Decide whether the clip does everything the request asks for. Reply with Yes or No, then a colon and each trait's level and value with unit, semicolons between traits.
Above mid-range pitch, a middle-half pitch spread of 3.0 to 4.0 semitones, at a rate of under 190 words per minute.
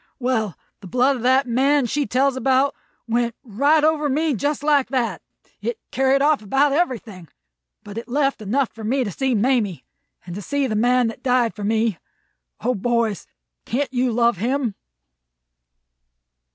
Yes: very high, 250 Hz; average, 3.5 semitones; average, 165 wpm